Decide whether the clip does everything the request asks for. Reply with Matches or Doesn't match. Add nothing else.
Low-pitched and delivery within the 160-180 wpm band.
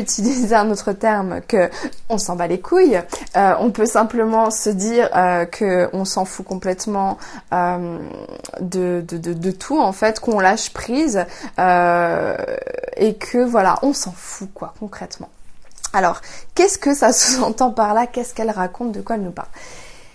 Doesn't match